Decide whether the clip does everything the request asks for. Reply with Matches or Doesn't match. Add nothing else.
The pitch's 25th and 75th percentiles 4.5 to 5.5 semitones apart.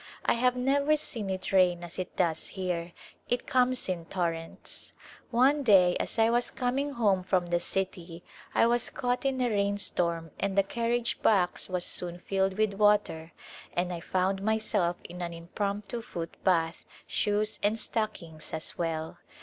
Matches